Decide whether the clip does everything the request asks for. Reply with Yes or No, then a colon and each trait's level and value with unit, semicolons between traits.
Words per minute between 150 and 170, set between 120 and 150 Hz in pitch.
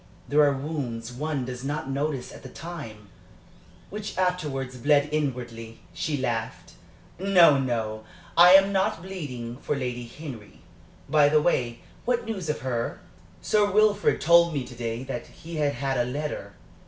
Yes: average, 160 wpm; medium, 140 Hz